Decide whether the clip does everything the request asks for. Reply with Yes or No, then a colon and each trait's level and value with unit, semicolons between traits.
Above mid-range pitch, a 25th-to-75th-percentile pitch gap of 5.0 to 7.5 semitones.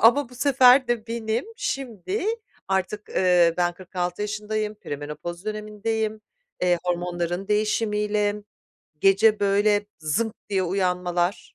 No: high, 210 Hz; average, 3.5 semitones